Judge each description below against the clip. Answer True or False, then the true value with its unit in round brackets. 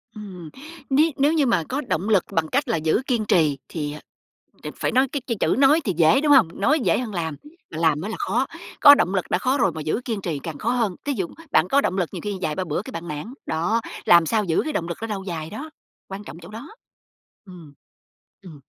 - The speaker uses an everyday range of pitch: False (7.4 semitones)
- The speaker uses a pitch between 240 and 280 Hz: False (195 Hz)